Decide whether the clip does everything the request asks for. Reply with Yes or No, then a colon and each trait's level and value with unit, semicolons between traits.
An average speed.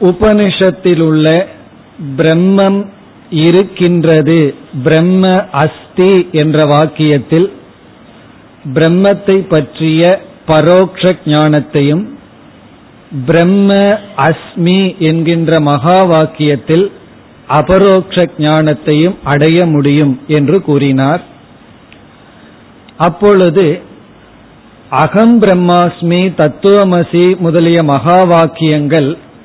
No: slow, 55 wpm